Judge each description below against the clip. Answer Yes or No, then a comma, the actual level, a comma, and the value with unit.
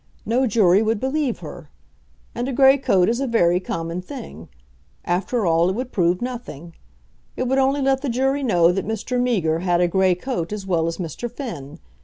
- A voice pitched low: No, high, 215 Hz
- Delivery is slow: No, average, 195 wpm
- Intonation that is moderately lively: No, wide, 6.5 semitones